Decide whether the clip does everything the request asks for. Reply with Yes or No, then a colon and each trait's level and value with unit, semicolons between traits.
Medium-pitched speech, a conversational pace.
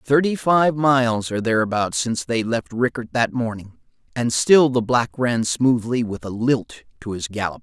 No: low, 115 Hz; average, 180 wpm